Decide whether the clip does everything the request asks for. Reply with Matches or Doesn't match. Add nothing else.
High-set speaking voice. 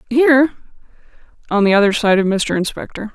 Matches